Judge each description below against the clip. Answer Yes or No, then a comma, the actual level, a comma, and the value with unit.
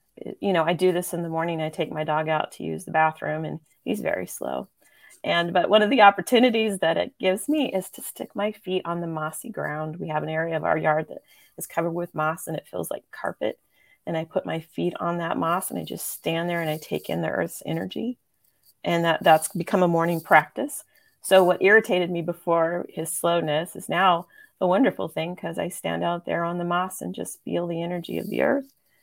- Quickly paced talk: Yes, fast, 230 wpm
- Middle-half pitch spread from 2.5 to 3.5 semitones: Yes, average, 2.9 semitones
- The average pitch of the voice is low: No, medium, 170 Hz